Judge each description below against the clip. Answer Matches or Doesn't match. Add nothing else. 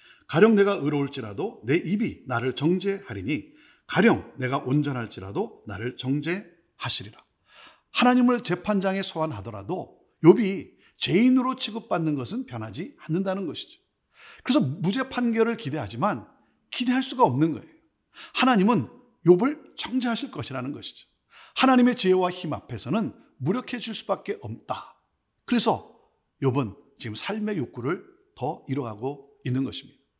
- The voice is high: Doesn't match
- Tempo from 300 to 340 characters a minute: Matches